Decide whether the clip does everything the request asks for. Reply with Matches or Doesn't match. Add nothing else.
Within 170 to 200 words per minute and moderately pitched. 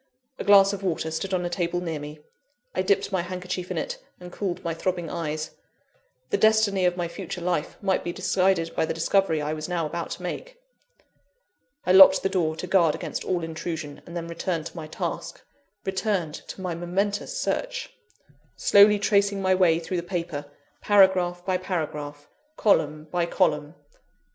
Matches